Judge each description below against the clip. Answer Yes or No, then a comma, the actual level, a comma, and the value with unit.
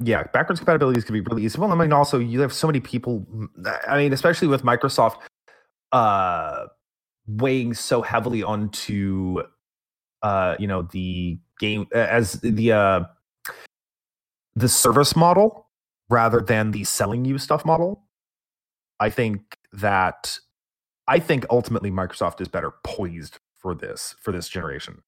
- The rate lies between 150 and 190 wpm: No, average, 140 wpm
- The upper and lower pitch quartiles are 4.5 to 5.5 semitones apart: Yes, average, 5.2 semitones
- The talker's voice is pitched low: Yes, low, 115 Hz